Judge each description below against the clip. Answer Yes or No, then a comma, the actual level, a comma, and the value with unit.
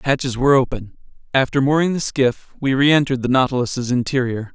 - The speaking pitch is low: Yes, low, 130 Hz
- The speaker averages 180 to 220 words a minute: No, average, 170 wpm